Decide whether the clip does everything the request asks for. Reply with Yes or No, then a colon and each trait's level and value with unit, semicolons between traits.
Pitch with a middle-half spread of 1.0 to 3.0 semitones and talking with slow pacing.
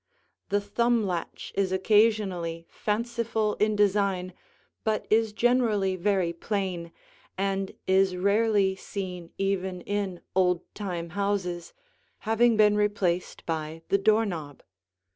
Yes: average, 2.7 semitones; slow, 115 wpm